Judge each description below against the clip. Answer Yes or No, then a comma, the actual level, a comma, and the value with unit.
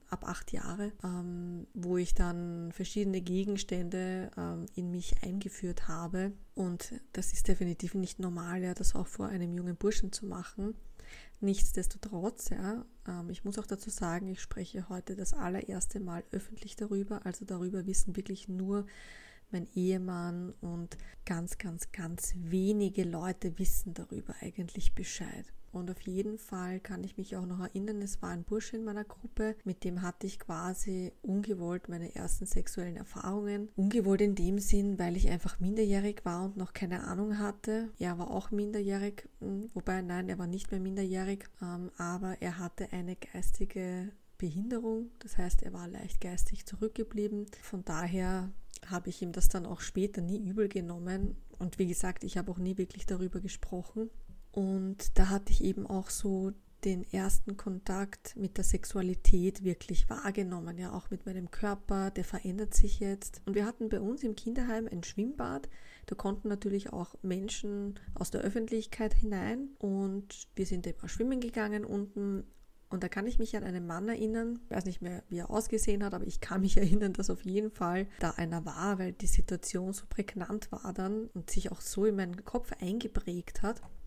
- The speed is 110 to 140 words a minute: No, average, 170 wpm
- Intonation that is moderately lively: No, narrow, 2.2 semitones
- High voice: Yes, high, 195 Hz